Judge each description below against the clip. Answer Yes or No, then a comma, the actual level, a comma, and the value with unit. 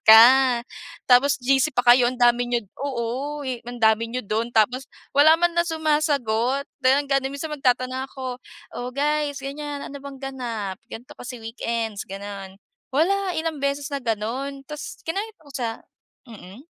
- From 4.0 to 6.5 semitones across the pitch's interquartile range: No, average, 3.3 semitones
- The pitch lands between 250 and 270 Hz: Yes, very high, 260 Hz